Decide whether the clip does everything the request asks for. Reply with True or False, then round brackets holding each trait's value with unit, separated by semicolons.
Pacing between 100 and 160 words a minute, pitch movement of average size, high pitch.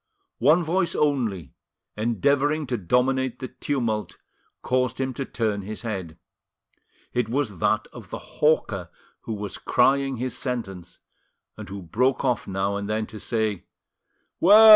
False (140 wpm; 4.7 semitones; 120 Hz)